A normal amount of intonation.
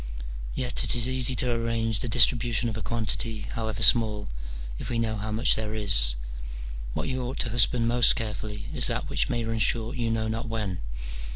No: narrow, 1.7 semitones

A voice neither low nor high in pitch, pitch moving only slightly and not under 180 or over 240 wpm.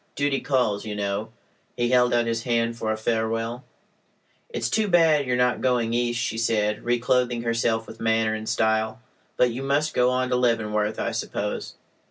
No: low, 115 Hz; narrow, 2.1 semitones; average, 185 wpm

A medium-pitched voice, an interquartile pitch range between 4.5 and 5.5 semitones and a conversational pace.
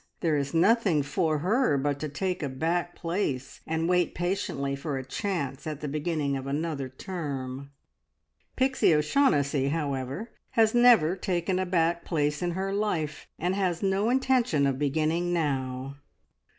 Yes: medium, 160 Hz; average, 5.0 semitones; average, 150 wpm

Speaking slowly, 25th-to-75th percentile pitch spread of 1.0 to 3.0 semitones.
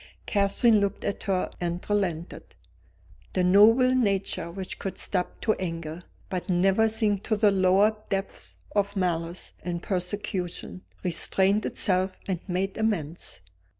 Yes: slow, 130 wpm; narrow, 2.4 semitones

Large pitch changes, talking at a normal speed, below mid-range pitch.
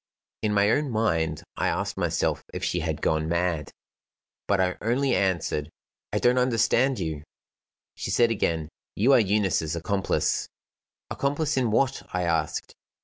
Yes: wide, 6.7 semitones; average, 145 wpm; low, 100 Hz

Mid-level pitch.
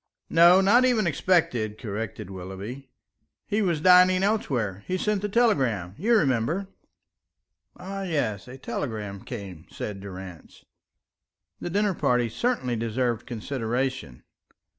No: low, 130 Hz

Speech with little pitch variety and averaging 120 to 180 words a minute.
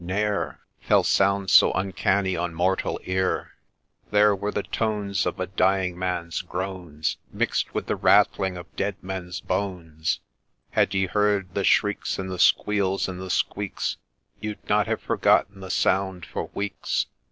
Yes: narrow, 1.7 semitones; average, 155 wpm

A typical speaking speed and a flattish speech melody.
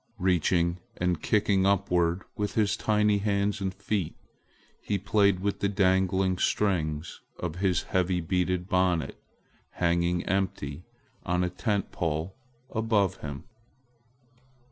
No: slow, 120 wpm; narrow, 2.3 semitones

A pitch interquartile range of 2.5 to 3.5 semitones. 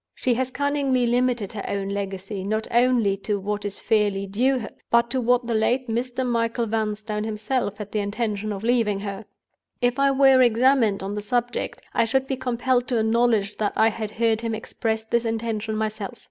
Yes: average, 2.8 semitones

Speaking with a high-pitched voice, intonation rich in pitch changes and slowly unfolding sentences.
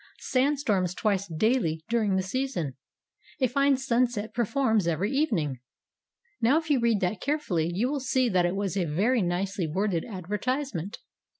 No: high, 210 Hz; wide, 6.1 semitones; average, 155 wpm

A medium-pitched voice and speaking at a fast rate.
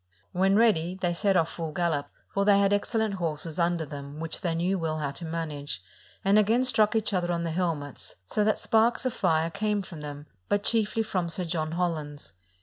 Yes: medium, 175 Hz; fast, 210 wpm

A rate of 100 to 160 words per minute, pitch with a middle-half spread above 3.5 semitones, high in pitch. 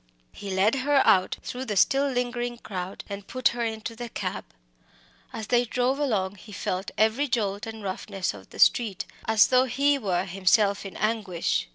No: average, 180 wpm; average, 4.0 semitones; high, 220 Hz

